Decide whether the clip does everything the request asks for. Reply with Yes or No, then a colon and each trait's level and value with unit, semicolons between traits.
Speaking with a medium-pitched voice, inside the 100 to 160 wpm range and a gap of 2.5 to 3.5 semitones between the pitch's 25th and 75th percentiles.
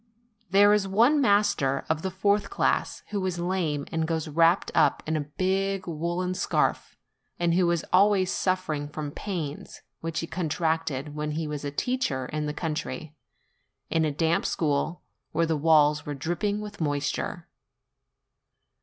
No: medium, 165 Hz; average, 155 wpm; average, 3.9 semitones